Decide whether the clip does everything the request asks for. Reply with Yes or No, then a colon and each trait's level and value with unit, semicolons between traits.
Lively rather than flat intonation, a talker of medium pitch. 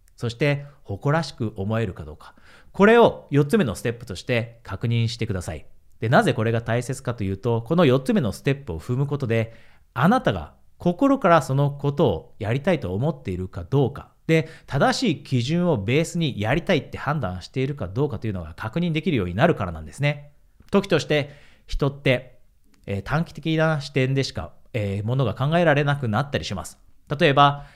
No: wide, 6.1 semitones; low, 130 Hz